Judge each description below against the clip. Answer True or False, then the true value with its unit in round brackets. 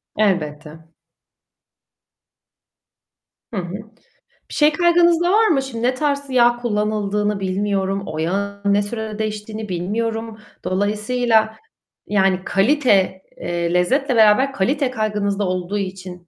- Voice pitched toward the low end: False (210 Hz)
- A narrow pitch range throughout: False (4.1 semitones)